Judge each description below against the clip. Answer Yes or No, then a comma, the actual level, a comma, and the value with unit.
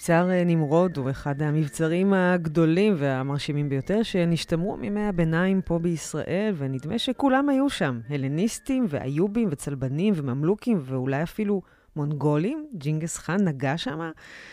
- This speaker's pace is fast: No, average, 115 wpm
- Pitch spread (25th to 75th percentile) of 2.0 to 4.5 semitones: No, wide, 5.4 semitones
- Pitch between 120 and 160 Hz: No, medium, 170 Hz